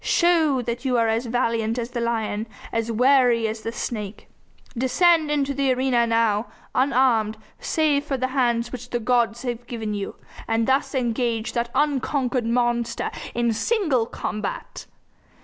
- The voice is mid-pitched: No, high, 240 Hz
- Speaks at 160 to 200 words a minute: No, average, 150 wpm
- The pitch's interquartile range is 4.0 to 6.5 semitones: No, narrow, 2.5 semitones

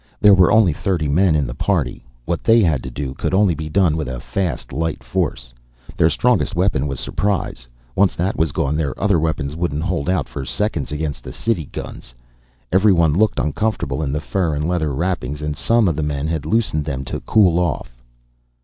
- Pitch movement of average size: Yes, average, 4.6 semitones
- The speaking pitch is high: No, very low, 80 Hz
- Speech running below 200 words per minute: No, fast, 205 wpm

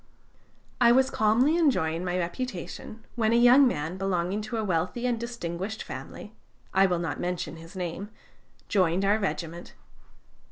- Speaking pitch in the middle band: No, high, 195 Hz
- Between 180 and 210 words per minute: No, average, 150 wpm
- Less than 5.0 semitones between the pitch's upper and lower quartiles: No, wide, 5.4 semitones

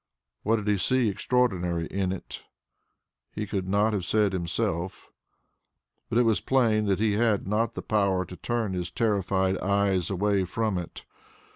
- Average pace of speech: Yes, average, 160 wpm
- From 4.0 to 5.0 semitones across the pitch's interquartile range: No, average, 2.8 semitones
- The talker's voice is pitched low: Yes, low, 100 Hz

